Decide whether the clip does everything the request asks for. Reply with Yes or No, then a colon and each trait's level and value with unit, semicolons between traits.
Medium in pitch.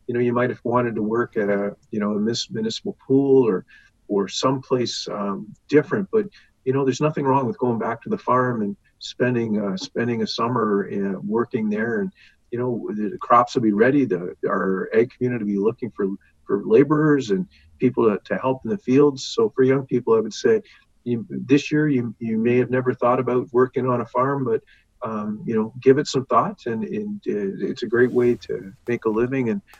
No: low, 125 Hz